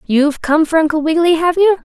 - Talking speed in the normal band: No, fast, 220 wpm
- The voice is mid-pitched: No, very high, 320 Hz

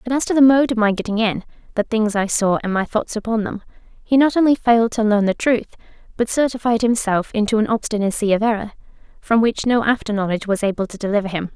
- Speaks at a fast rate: Yes, fast, 230 wpm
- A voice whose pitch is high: Yes, high, 220 Hz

